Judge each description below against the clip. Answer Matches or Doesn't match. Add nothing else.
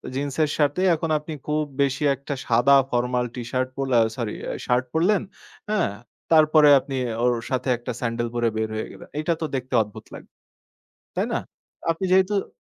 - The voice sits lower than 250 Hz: Matches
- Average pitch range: Matches